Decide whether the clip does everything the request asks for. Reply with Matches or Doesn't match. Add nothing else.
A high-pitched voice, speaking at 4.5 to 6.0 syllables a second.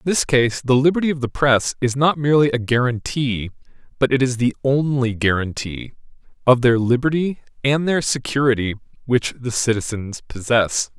Doesn't match